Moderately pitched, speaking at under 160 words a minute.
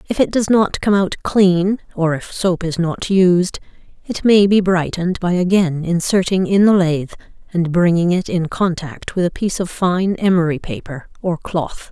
No: medium, 180 Hz; average, 185 wpm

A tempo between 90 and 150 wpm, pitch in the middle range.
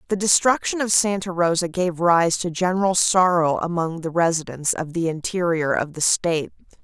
No: average, 165 wpm; medium, 175 Hz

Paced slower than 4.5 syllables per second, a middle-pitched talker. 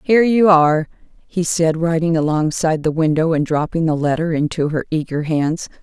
No: 5.4 syllables/s; medium, 160 Hz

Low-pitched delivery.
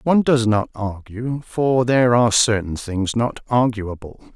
Yes: low, 115 Hz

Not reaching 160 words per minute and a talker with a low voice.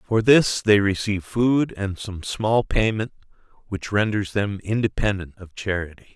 Yes: average, 145 wpm; low, 105 Hz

